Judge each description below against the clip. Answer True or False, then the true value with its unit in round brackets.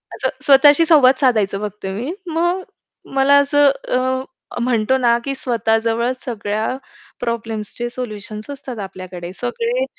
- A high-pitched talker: True (245 Hz)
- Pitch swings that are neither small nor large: True (4.4 semitones)